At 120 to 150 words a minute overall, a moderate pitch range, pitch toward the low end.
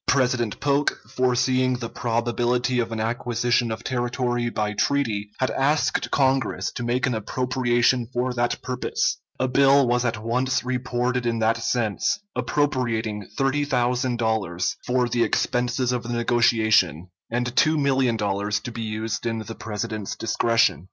No: average, 140 wpm; narrow, 2.1 semitones; low, 120 Hz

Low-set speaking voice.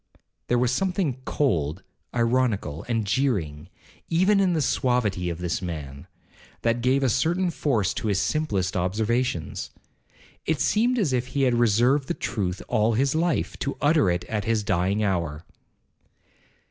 Yes: low, 115 Hz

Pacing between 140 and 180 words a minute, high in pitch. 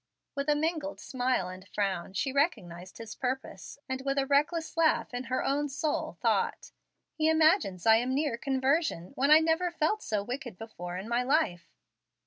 Yes: average, 175 wpm; very high, 265 Hz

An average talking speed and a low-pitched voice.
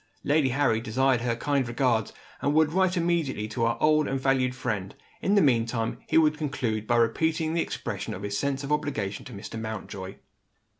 Yes: average, 190 wpm; low, 130 Hz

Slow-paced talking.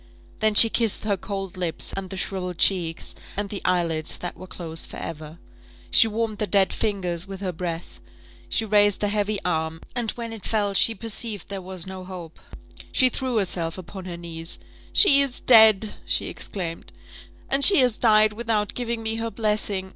No: average, 185 wpm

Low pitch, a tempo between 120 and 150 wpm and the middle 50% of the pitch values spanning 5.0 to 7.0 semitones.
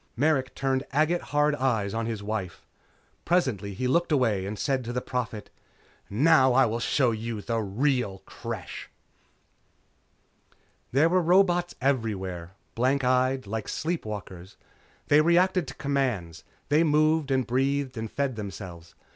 Yes: low, 130 Hz; average, 140 wpm; average, 5.3 semitones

